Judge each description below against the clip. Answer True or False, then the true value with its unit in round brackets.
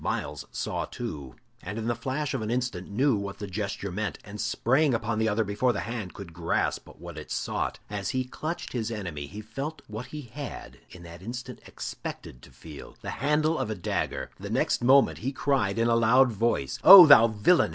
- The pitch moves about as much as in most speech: True (4.5 semitones)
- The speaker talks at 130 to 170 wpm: False (205 wpm)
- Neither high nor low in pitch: False (110 Hz)